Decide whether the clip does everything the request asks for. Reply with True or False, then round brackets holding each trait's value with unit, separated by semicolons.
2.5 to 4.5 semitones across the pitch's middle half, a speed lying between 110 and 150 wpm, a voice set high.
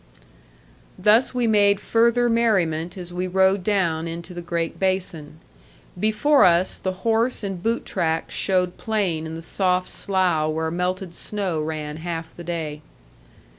False (3.7 semitones; 145 wpm; 180 Hz)